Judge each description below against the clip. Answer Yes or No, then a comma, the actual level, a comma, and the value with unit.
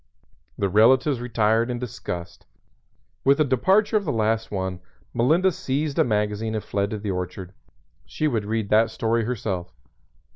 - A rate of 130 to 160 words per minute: Yes, average, 155 wpm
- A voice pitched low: Yes, low, 115 Hz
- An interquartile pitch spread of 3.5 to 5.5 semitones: Yes, average, 4.1 semitones